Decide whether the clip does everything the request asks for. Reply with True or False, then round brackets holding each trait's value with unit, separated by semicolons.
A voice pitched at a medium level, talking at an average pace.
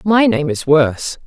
True (165 Hz; 190 wpm)